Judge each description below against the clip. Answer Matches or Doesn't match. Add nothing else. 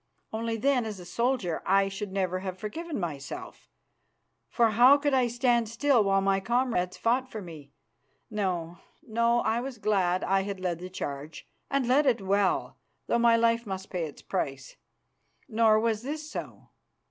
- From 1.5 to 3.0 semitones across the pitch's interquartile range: Doesn't match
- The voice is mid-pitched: Doesn't match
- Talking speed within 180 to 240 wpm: Doesn't match